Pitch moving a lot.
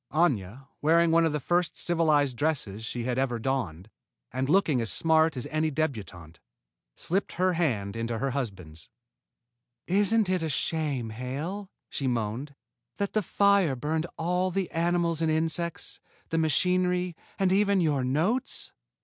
Yes: wide, 5.7 semitones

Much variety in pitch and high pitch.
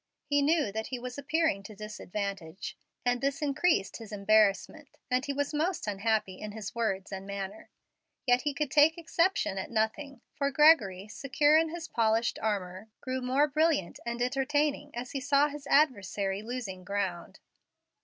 Yes: wide, 6.2 semitones; high, 245 Hz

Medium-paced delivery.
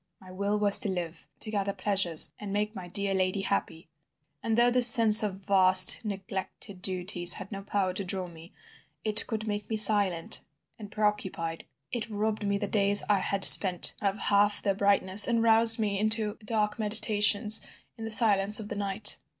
Yes: average, 180 wpm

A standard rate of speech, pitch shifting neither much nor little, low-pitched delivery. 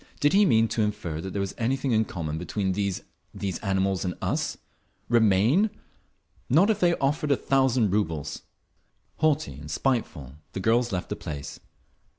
No: average, 155 wpm; wide, 6.2 semitones; low, 105 Hz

